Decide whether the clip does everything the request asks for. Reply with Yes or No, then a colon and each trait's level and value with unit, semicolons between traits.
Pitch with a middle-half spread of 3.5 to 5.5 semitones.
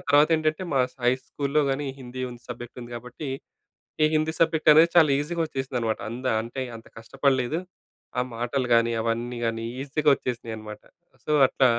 Yes: average, 3.9 semitones